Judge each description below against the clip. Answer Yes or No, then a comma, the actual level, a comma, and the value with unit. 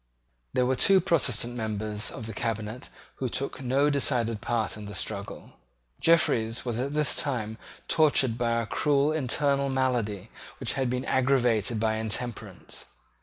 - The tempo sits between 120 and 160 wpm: Yes, average, 150 wpm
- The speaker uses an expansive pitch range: No, average, 3.8 semitones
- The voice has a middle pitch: No, low, 120 Hz